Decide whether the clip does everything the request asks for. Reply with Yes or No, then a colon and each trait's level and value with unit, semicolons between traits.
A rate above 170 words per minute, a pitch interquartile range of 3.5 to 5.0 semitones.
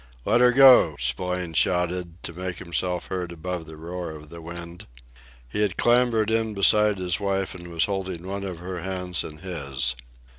No: average, 180 wpm; narrow, 2.5 semitones